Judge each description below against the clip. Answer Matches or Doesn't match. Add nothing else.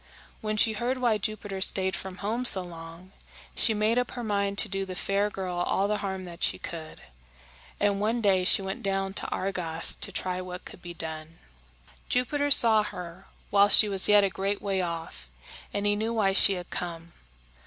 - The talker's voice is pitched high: Matches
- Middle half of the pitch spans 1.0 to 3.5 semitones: Matches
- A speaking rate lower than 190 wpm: Doesn't match